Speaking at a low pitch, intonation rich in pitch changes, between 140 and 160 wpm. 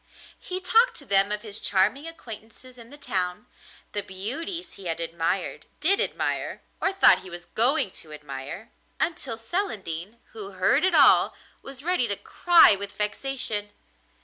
No: high, 220 Hz; wide, 7.3 semitones; average, 155 wpm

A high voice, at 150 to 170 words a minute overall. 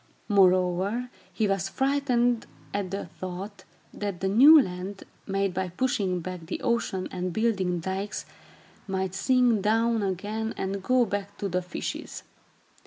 No: high, 195 Hz; average, 140 wpm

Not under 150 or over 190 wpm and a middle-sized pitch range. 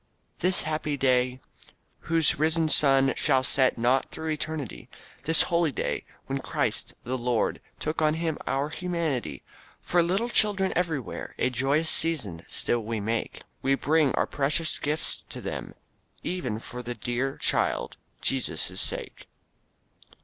No: average, 140 wpm; average, 4.3 semitones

